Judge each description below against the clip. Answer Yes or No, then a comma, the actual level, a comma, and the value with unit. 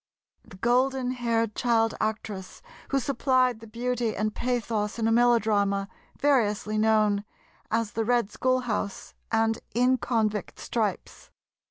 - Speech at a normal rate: No, slow, 125 wpm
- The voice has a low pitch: No, high, 225 Hz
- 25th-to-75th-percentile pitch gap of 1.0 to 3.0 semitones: Yes, narrow, 2.5 semitones